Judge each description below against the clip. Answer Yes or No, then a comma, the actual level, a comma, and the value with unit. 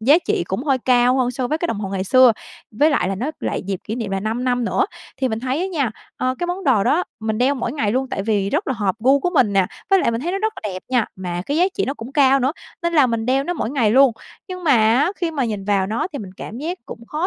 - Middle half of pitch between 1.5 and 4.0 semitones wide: No, average, 5.1 semitones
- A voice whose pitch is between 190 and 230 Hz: No, very high, 255 Hz